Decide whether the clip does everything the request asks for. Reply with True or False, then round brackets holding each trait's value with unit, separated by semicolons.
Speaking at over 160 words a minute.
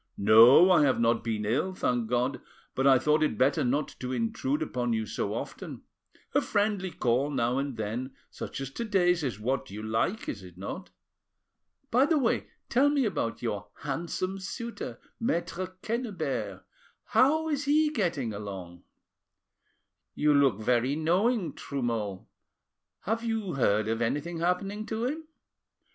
False (155 wpm)